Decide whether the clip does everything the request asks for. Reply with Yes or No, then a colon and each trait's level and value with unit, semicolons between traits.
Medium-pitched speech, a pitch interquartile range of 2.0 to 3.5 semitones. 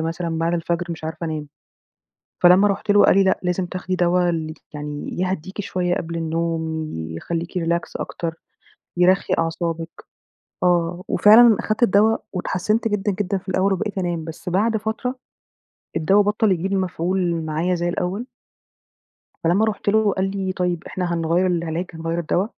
Yes: medium, 180 Hz; average, 2.8 semitones